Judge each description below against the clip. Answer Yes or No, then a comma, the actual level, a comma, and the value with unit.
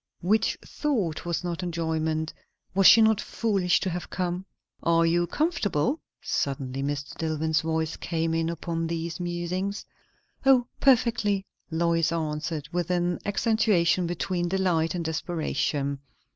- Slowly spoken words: Yes, slow, 130 wpm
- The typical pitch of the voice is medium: Yes, medium, 170 Hz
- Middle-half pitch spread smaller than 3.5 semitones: Yes, average, 2.9 semitones